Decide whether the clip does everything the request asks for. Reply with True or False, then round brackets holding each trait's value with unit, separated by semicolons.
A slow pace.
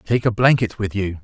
False (245 wpm)